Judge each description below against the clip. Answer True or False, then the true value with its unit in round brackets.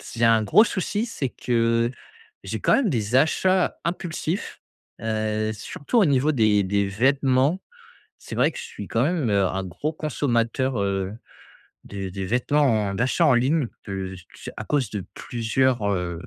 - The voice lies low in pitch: True (120 Hz)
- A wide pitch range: True (6.2 semitones)